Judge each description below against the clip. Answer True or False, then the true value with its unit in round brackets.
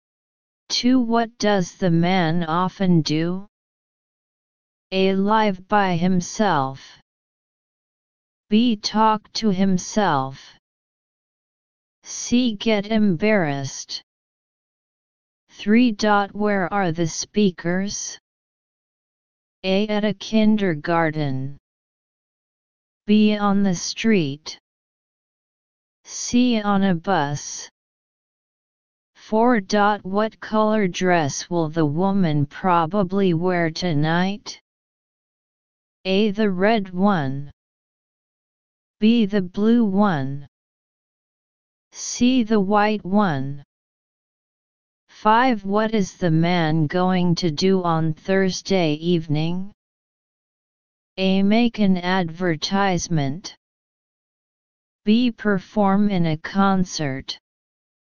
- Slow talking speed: True (80 wpm)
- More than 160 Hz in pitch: True (190 Hz)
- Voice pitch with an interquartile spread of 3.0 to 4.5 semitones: True (3.7 semitones)